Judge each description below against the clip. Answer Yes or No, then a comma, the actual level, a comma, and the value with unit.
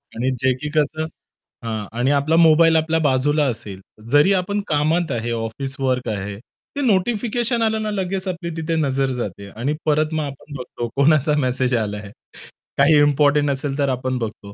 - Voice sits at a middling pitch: Yes, medium, 145 Hz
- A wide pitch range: No, average, 4.3 semitones